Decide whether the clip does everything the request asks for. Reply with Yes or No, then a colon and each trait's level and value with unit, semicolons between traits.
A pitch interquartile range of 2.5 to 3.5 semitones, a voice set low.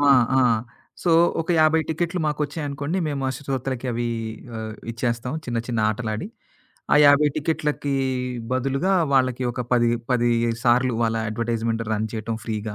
No: average, 3.9 semitones; low, 130 Hz